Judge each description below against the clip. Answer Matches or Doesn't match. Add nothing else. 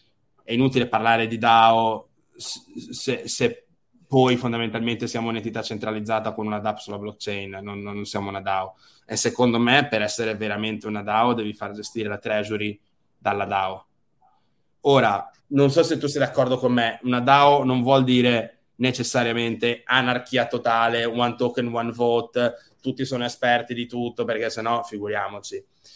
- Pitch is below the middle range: Matches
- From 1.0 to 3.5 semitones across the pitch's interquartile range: Matches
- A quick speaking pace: Doesn't match